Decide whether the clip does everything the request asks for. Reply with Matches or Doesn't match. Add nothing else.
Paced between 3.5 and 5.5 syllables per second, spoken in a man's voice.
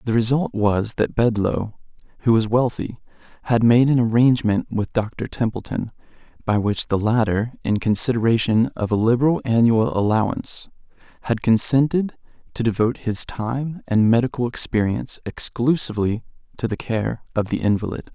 Matches